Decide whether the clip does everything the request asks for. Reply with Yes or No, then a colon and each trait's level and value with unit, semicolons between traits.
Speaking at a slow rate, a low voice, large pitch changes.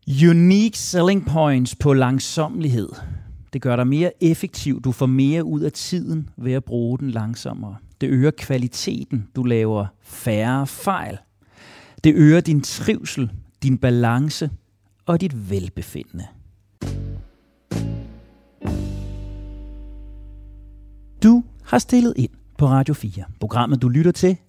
Yes: slow, 120 wpm; low, 125 Hz; wide, 7.1 semitones